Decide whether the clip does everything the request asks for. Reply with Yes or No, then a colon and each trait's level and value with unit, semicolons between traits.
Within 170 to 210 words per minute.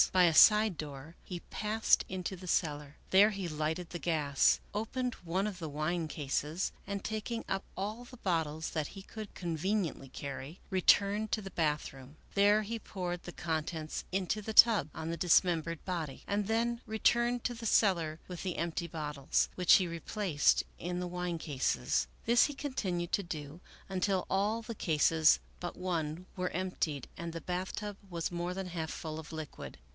Yes: average, 175 wpm